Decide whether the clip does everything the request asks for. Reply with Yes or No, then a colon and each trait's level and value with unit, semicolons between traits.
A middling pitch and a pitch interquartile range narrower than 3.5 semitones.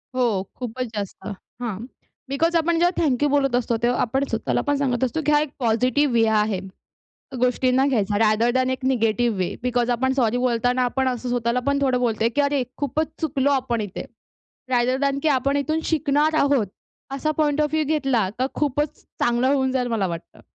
No: very high, 255 Hz; average, 3.1 semitones